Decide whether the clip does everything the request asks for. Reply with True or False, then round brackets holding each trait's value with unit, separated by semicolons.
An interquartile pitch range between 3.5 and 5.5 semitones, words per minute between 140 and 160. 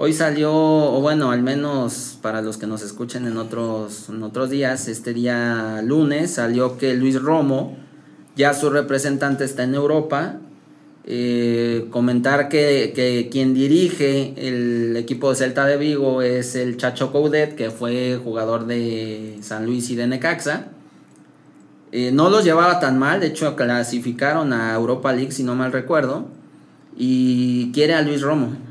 False (3.1 semitones; 155 wpm)